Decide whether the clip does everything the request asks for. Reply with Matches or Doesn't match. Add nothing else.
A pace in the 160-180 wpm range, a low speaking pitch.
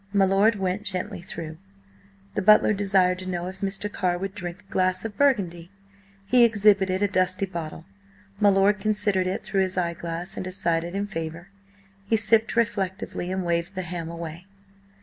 Doesn't match